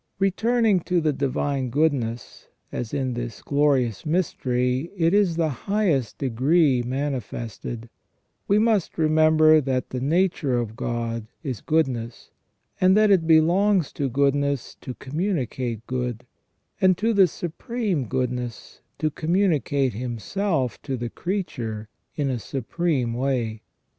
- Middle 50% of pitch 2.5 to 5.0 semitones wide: No, wide, 5.6 semitones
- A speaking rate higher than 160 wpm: No, slow, 135 wpm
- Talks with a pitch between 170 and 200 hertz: No, medium, 140 Hz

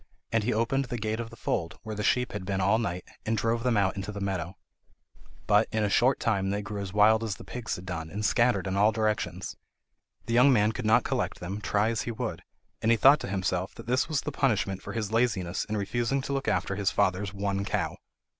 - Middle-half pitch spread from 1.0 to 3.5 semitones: Yes, average, 2.9 semitones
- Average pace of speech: No, fast, 240 wpm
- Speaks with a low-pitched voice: Yes, low, 105 Hz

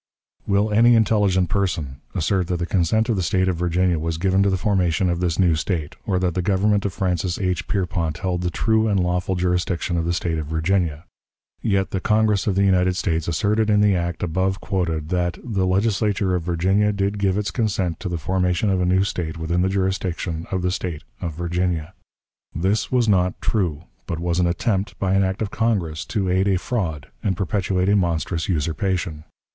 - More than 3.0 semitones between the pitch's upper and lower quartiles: No, narrow, 2.5 semitones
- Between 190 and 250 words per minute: Yes, fast, 205 wpm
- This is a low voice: Yes, very low, 90 Hz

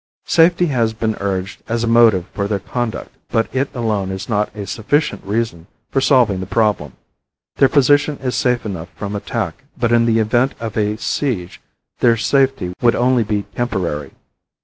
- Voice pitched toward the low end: Yes, low, 115 Hz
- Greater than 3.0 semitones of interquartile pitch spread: Yes, average, 3.6 semitones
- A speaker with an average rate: Yes, average, 170 wpm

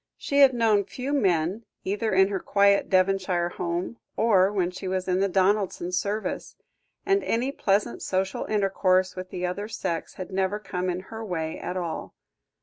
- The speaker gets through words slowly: No, average, 170 wpm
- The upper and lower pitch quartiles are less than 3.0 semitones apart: Yes, narrow, 2.4 semitones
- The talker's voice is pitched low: No, high, 190 Hz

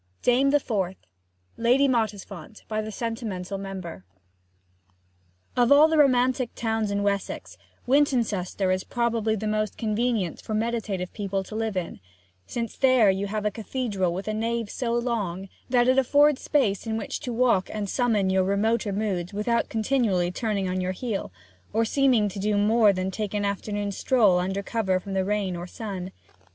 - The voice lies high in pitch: Yes, high, 215 Hz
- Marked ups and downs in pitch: No, average, 3.4 semitones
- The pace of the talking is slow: No, average, 170 wpm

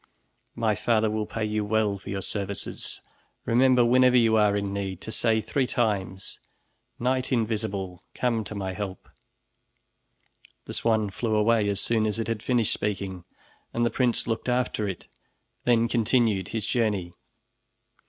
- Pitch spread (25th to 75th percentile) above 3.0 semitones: No, narrow, 2.6 semitones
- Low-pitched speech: Yes, low, 110 Hz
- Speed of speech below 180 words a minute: Yes, average, 155 wpm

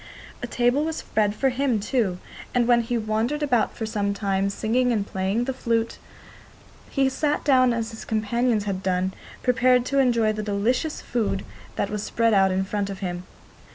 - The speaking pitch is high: Yes, high, 225 Hz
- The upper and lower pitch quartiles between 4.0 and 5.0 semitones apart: No, average, 3.6 semitones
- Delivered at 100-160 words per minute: No, average, 190 wpm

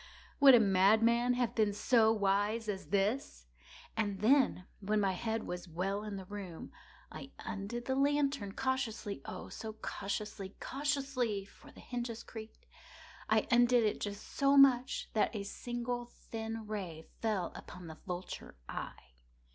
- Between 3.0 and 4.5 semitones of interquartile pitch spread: Yes, average, 3.5 semitones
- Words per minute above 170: No, average, 140 wpm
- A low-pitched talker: No, high, 220 Hz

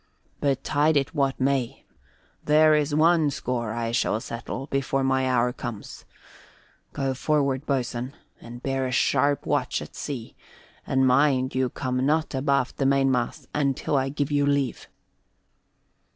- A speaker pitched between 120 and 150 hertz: Yes, low, 135 Hz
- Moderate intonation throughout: No, narrow, 2.0 semitones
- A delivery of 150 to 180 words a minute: No, average, 140 wpm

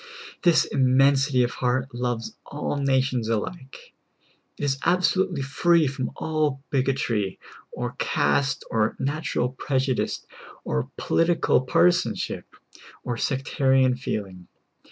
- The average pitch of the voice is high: No, low, 135 Hz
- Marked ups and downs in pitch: No, average, 2.7 semitones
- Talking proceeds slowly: Yes, slow, 110 wpm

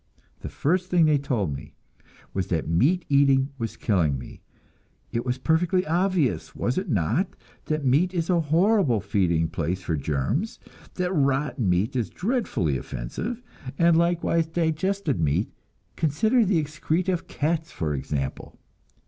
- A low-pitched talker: No, medium, 145 Hz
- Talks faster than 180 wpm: No, average, 145 wpm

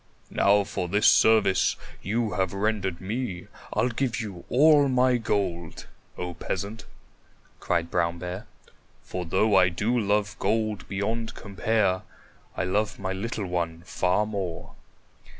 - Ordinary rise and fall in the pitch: Yes, average, 3.4 semitones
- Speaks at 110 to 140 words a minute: Yes, slow, 135 wpm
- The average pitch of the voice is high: No, low, 100 Hz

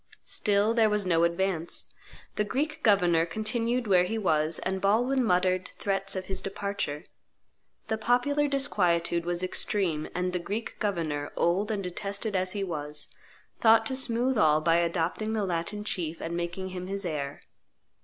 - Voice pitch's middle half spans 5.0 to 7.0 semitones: No, average, 4.1 semitones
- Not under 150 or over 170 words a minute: Yes, average, 160 wpm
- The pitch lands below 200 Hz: Yes, high, 190 Hz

